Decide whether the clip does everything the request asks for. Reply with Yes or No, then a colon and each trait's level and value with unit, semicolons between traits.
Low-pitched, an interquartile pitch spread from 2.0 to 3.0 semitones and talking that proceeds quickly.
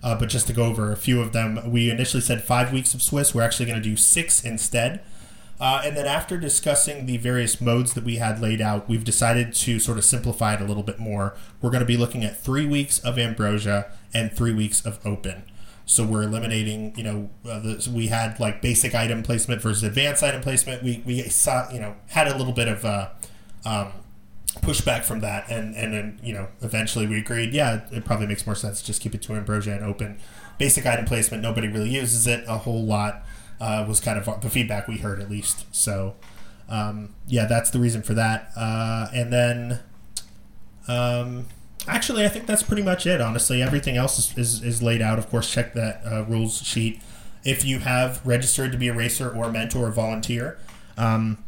Yes: low, 115 Hz; narrow, 2.4 semitones; fast, 220 wpm